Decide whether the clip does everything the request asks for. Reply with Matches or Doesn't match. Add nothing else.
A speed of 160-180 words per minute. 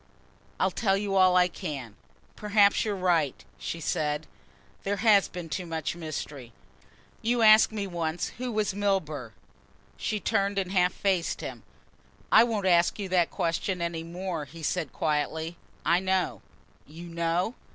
Doesn't match